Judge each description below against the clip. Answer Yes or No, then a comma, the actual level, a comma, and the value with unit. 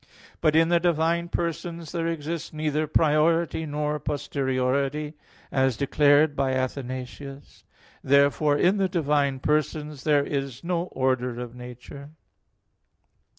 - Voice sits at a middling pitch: Yes, medium, 150 Hz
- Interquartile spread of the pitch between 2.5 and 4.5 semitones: Yes, average, 3.1 semitones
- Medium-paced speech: No, slow, 115 wpm